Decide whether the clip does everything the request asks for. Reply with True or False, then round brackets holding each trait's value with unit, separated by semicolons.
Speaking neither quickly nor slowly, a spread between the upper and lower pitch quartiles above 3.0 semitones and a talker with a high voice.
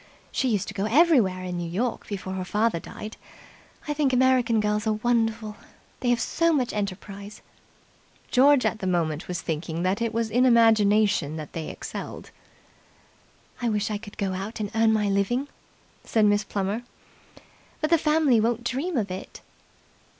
True (170 wpm; 3.6 semitones; 215 Hz)